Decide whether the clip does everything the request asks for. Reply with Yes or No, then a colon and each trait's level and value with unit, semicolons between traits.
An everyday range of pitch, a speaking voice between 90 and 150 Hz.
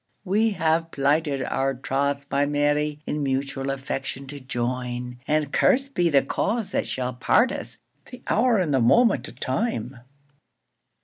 Yes: average, 4.1 semitones; medium, 140 Hz